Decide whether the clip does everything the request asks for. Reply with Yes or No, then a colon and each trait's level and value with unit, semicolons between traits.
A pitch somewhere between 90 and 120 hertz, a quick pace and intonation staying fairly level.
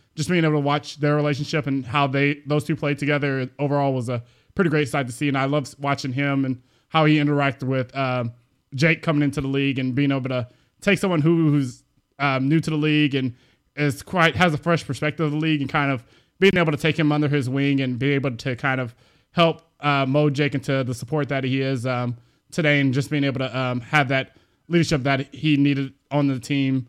No: medium, 140 Hz; fast, 235 wpm; narrow, 2.1 semitones